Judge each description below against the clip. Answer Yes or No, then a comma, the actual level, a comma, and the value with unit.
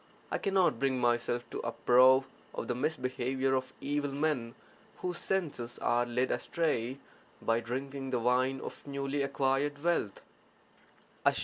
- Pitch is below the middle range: Yes, low, 130 Hz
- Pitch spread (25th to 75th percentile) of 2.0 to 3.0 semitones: Yes, average, 2.7 semitones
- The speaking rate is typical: No, slow, 130 wpm